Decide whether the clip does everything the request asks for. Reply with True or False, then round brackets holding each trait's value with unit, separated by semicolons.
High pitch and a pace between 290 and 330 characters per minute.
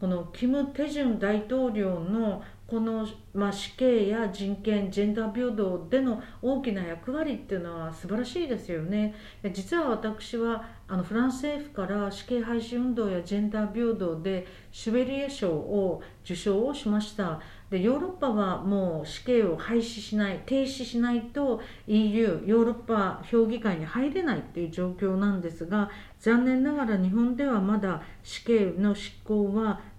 True (215 Hz; 315 characters per minute)